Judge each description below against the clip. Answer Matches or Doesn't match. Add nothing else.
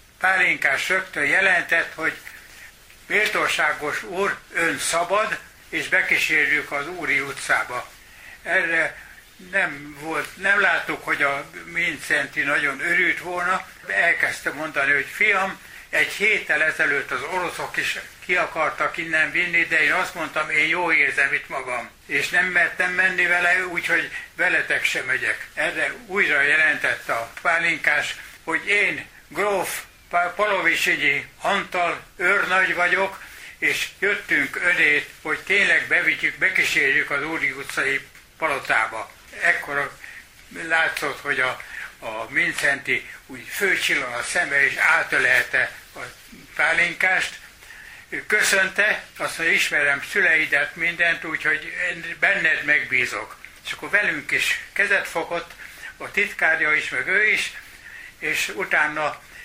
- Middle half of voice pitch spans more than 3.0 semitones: Doesn't match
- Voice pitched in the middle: Matches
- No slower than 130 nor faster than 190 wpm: Doesn't match